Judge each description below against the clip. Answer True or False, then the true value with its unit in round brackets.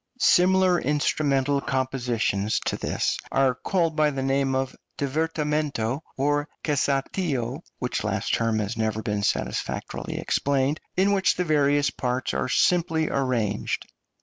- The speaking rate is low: True (125 wpm)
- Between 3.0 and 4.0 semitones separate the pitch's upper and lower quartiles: True (3.4 semitones)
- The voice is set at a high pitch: False (140 Hz)